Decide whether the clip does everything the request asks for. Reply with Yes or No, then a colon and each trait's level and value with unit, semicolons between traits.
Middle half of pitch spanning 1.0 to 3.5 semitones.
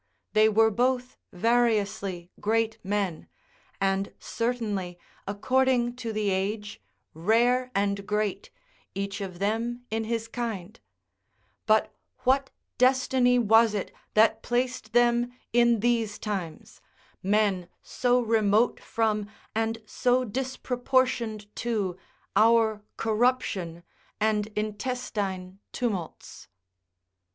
Yes: average, 3.1 semitones